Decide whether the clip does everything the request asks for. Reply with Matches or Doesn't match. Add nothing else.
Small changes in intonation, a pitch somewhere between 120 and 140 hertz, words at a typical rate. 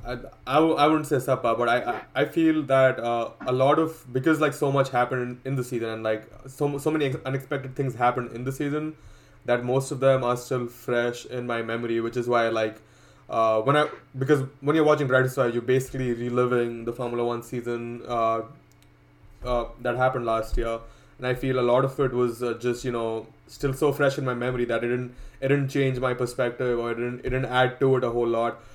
Doesn't match